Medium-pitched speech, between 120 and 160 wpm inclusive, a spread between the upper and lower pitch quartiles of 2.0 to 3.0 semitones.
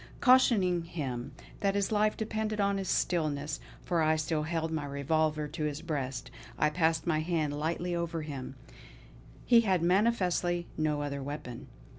No: medium, 160 Hz; average, 155 wpm; average, 3.5 semitones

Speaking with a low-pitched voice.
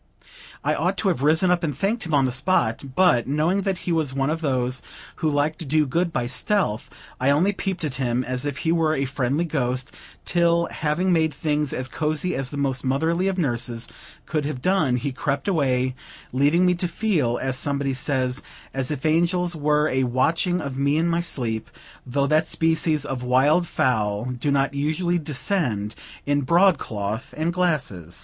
No: medium, 145 Hz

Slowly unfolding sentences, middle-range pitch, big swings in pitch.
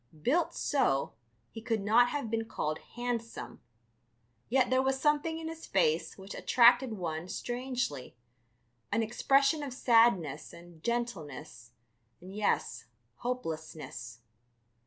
No: slow, 115 wpm; high, 230 Hz; wide, 7.1 semitones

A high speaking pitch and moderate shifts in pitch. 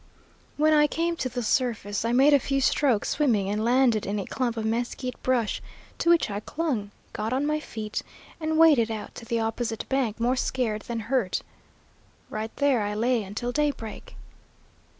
Yes: high, 240 Hz; average, 4.0 semitones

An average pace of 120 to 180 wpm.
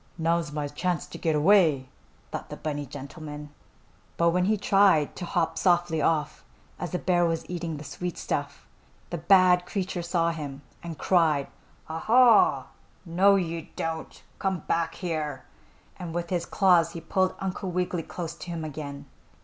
Yes: average, 165 wpm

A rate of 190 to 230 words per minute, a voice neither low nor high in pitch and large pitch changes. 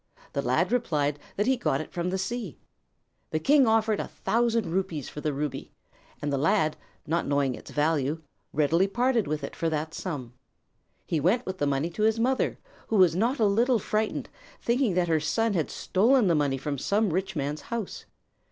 Yes: average, 195 wpm; medium, 180 Hz; wide, 6.9 semitones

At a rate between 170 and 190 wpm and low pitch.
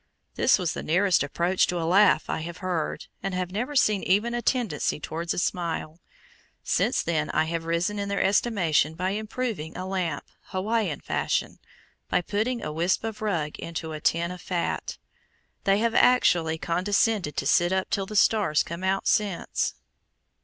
No: average, 175 wpm; medium, 185 Hz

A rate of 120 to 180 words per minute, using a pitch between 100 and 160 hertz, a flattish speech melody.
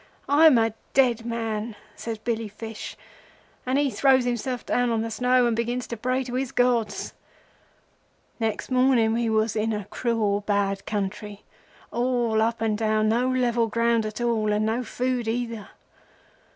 No: average, 155 wpm; high, 230 Hz; narrow, 2.1 semitones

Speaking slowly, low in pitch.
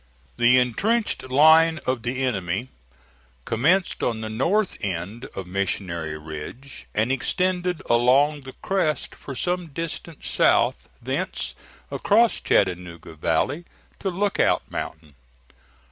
Yes: slow, 115 wpm; low, 130 Hz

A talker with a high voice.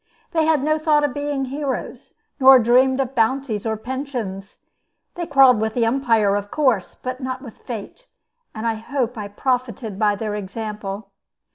Yes: high, 245 Hz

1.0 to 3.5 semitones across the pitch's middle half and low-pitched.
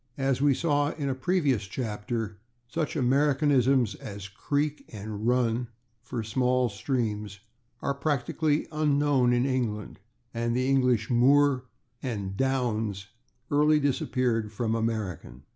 No: average, 4.2 semitones; low, 125 Hz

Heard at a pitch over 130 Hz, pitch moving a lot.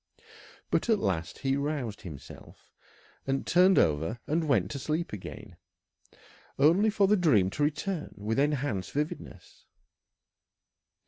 Yes: medium, 140 Hz; wide, 8.3 semitones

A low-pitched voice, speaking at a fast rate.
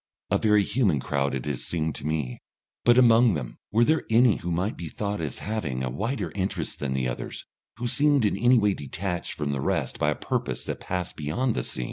Yes: very low, 90 Hz; fast, 225 wpm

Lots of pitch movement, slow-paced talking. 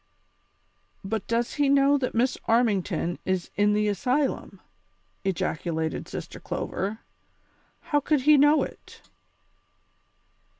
Yes: wide, 6.2 semitones; slow, 110 wpm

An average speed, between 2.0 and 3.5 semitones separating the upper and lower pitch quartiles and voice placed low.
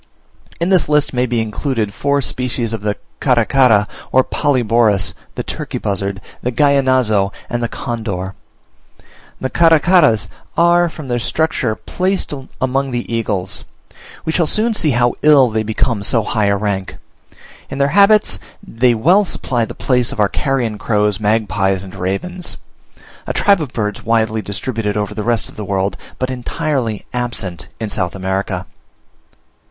No: average, 155 wpm; average, 5.0 semitones; low, 120 Hz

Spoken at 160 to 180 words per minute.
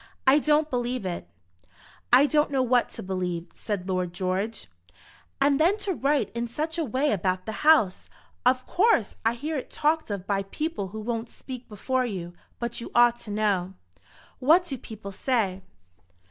Yes: average, 175 wpm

